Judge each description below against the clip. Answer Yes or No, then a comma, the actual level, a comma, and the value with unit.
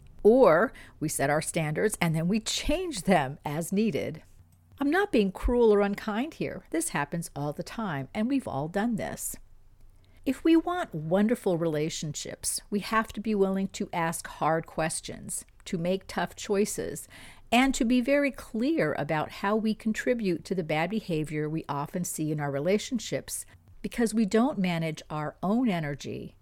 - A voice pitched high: Yes, high, 195 Hz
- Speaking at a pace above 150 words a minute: Yes, average, 165 wpm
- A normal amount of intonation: No, wide, 5.9 semitones